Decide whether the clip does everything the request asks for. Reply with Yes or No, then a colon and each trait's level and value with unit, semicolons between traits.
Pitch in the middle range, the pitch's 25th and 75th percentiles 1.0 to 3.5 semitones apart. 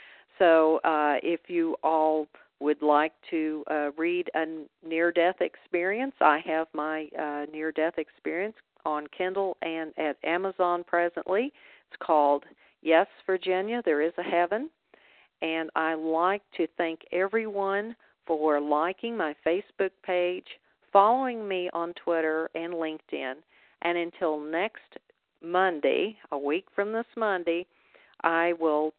Yes: medium, 170 Hz; average, 2.8 semitones